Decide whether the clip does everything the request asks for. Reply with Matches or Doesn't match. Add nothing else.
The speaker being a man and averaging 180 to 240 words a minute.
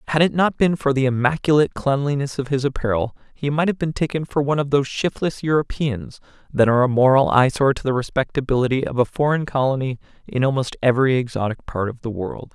Matches